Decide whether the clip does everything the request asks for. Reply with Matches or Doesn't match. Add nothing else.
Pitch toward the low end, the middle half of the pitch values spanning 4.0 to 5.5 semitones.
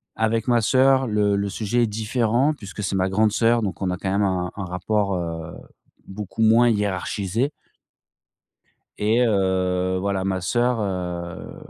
Doesn't match